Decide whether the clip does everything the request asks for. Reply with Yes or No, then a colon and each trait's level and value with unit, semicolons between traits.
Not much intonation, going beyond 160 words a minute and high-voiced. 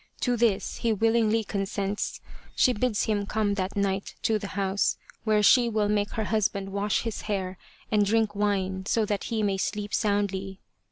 Yes: narrow, 1.8 semitones; average, 180 wpm; high, 205 Hz